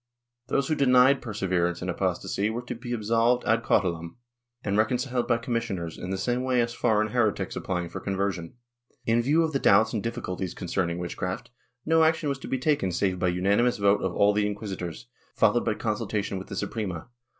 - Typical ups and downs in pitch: Yes, average, 4.8 semitones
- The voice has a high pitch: No, low, 105 Hz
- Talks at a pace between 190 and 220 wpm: Yes, average, 195 wpm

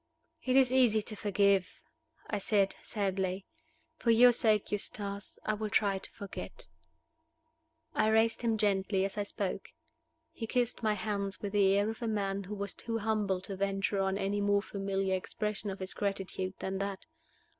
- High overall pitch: Yes, high, 200 Hz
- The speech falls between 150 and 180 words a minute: Yes, average, 170 wpm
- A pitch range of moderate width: No, narrow, 1.7 semitones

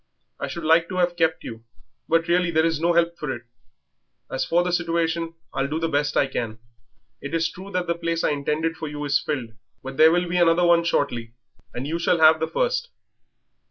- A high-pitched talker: No, medium, 165 Hz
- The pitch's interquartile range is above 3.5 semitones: No, average, 2.7 semitones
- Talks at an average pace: No, fast, 215 wpm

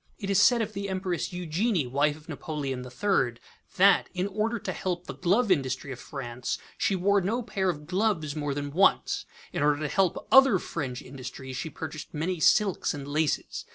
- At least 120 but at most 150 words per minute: No, average, 190 wpm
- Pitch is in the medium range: Yes, medium, 165 Hz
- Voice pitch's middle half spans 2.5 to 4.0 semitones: No, wide, 5.5 semitones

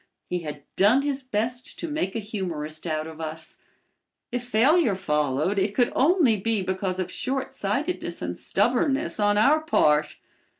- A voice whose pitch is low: No, high, 205 Hz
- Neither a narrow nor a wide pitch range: No, wide, 7.6 semitones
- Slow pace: No, average, 155 wpm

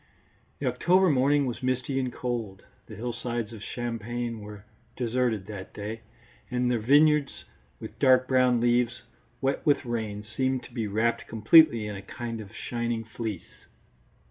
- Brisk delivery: No, average, 150 wpm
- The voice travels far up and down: No, narrow, 2.6 semitones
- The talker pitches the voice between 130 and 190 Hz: No, low, 120 Hz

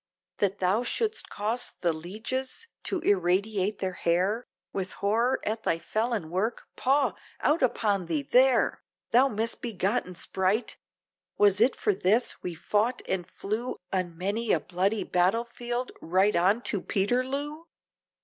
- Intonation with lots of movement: No, average, 4.5 semitones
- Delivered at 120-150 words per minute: Yes, average, 140 wpm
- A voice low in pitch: No, high, 210 Hz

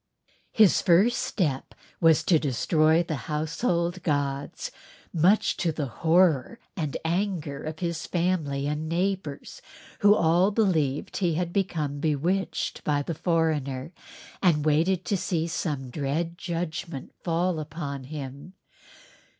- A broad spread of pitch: No, average, 3.4 semitones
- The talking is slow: Yes, slow, 125 wpm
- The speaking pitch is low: No, medium, 160 Hz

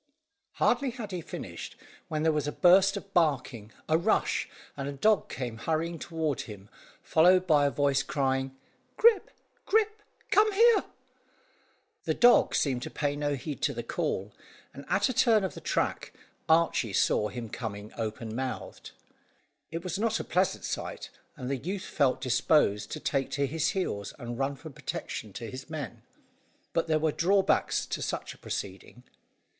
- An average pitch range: No, wide, 6.3 semitones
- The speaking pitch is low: No, medium, 150 Hz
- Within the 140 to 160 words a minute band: No, average, 170 wpm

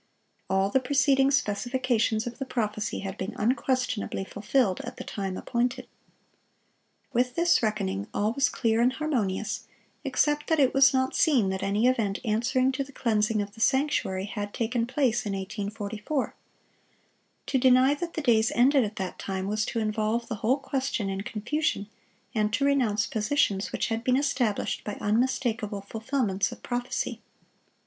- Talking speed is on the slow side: No, average, 160 wpm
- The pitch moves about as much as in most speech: Yes, average, 4.0 semitones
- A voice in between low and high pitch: No, high, 230 Hz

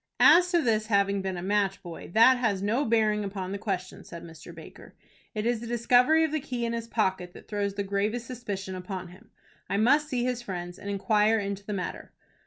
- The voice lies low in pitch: No, high, 210 Hz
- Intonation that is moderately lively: Yes, average, 3.7 semitones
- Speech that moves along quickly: Yes, fast, 215 wpm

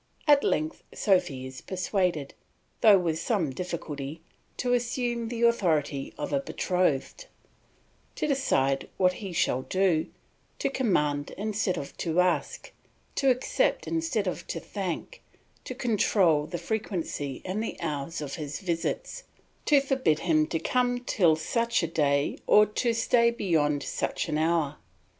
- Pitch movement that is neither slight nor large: No, wide, 7.1 semitones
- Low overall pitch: No, medium, 180 Hz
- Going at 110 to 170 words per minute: Yes, average, 145 wpm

